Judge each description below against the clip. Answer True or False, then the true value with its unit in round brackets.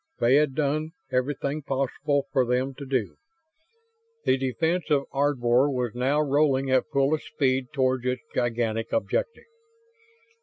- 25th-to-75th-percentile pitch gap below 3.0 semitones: True (2.4 semitones)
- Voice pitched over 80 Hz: True (135 Hz)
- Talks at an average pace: False (130 wpm)